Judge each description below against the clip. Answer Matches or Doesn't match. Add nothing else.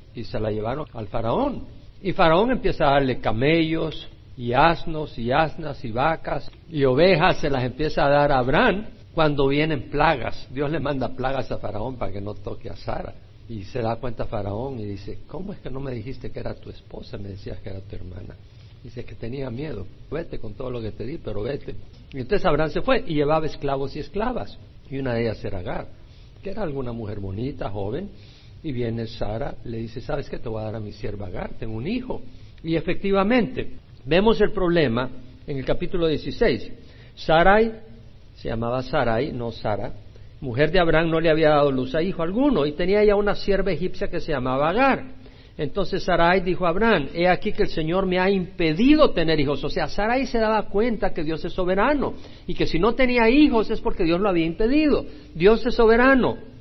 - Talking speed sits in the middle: Doesn't match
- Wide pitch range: Matches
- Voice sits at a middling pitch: Matches